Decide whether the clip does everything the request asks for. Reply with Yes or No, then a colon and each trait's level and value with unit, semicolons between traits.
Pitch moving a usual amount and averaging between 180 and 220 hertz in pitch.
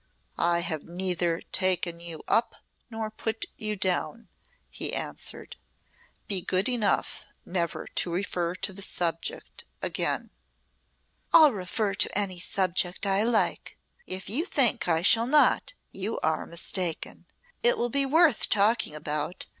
Yes: average, 4.4 semitones; high, 190 Hz